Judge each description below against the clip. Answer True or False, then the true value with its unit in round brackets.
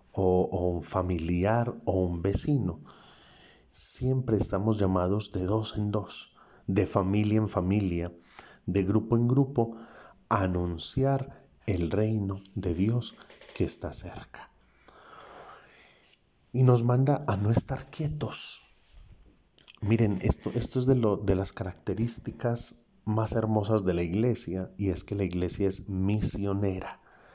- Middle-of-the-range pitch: False (105 Hz)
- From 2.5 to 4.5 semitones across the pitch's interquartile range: True (3.6 semitones)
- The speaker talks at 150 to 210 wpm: False (130 wpm)